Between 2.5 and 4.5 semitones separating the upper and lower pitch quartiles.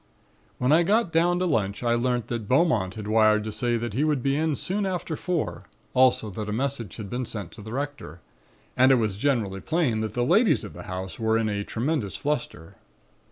No: wide, 5.5 semitones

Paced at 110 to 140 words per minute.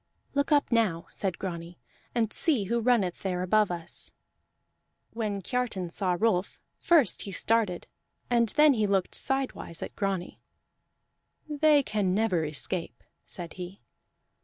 Yes: slow, 135 wpm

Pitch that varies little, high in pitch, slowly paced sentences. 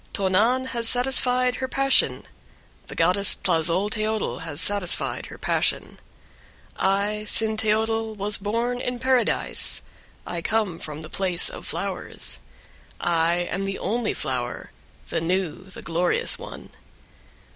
No: average, 4.5 semitones; high, 205 Hz; slow, 125 wpm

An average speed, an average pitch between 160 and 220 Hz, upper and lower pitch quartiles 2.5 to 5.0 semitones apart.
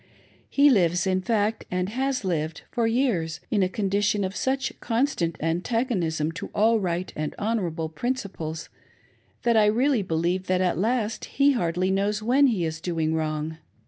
No: average, 165 wpm; high, 190 Hz; wide, 5.5 semitones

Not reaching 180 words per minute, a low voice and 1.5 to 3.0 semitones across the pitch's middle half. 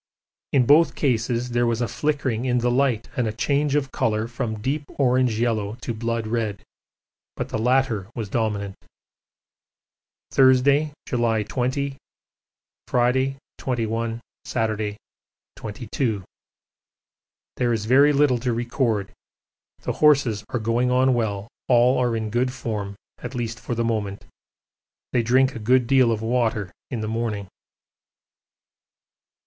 Yes: slow, 135 wpm; low, 120 Hz; average, 2.7 semitones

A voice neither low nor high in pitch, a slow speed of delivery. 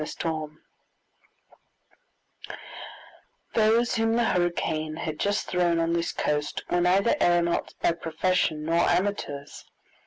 Yes: medium, 170 Hz; slow, 115 wpm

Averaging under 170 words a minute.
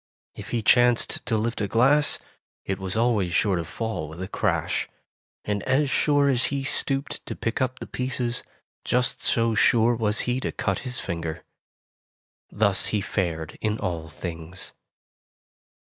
Yes: average, 160 wpm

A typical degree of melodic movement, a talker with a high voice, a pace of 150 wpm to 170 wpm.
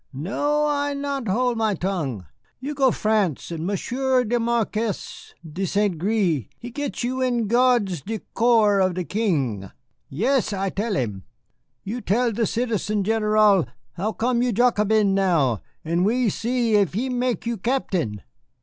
Yes: average, 4.5 semitones; high, 215 Hz; average, 155 wpm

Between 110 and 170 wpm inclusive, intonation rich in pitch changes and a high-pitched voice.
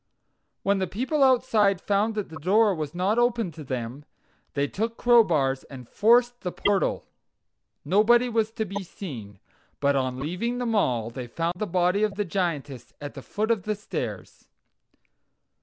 Yes: average, 165 wpm; wide, 7.4 semitones; high, 195 Hz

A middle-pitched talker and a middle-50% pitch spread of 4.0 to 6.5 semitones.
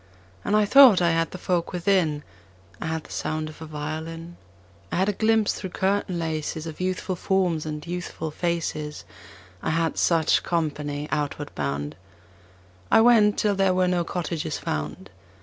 No: medium, 165 Hz; average, 3.2 semitones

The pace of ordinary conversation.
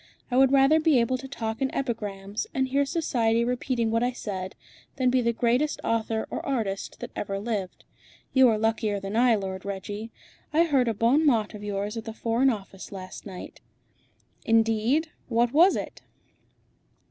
Yes: average, 175 wpm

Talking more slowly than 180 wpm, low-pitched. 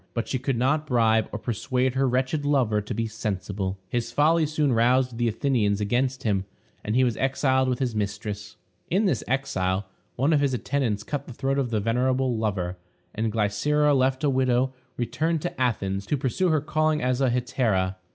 No: average, 190 wpm; low, 125 Hz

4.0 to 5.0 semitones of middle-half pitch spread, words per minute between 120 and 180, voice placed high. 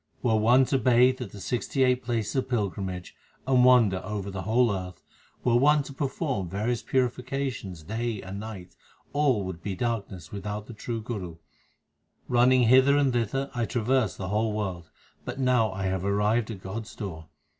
No: average, 4.4 semitones; average, 175 wpm; low, 115 Hz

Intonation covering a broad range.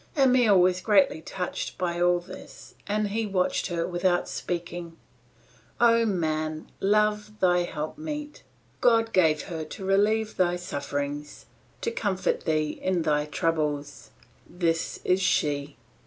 No: average, 4.7 semitones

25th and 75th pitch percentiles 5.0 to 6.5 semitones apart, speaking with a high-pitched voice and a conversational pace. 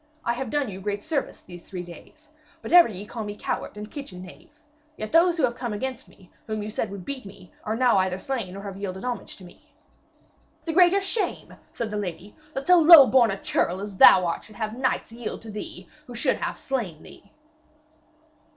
No: wide, 5.4 semitones; high, 215 Hz; fast, 215 wpm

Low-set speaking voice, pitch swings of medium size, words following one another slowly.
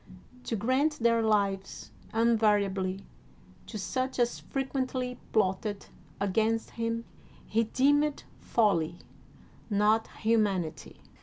No: high, 225 Hz; average, 3.3 semitones; slow, 90 wpm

